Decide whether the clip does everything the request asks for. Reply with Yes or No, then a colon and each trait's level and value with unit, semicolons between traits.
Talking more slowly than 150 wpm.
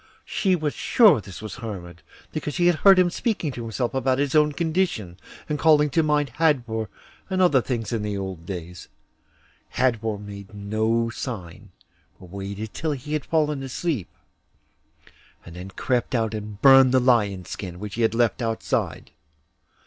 No: average, 165 wpm